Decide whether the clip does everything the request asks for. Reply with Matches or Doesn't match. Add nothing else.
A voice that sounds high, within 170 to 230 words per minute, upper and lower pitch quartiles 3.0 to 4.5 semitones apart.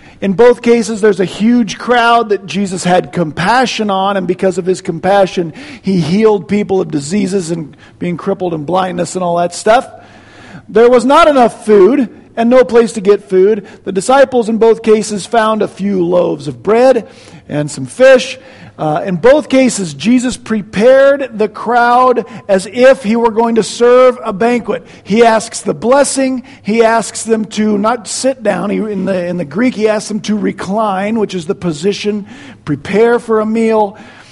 Matches